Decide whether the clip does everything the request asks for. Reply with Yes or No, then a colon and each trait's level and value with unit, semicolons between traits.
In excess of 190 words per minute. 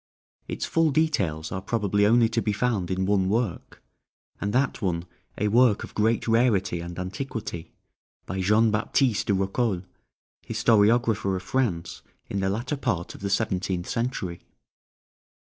No: average, 145 wpm